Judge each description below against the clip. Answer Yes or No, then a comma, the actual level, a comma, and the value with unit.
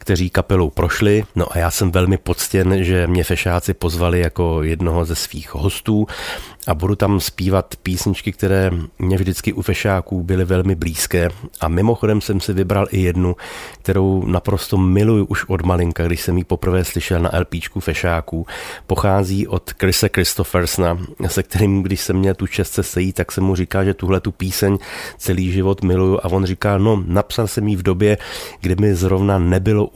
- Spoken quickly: Yes, fast, 175 wpm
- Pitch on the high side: No, very low, 95 Hz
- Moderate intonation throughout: No, narrow, 1.9 semitones